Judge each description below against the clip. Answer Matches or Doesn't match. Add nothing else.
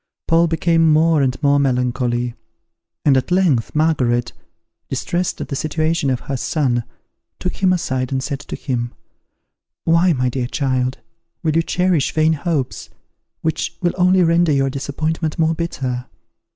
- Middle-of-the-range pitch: Matches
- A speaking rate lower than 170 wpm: Matches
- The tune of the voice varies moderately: Matches